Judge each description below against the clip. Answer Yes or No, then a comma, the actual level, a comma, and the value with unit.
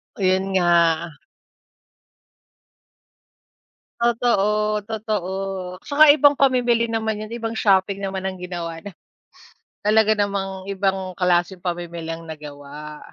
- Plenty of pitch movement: No, average, 3.9 semitones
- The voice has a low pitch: No, high, 195 Hz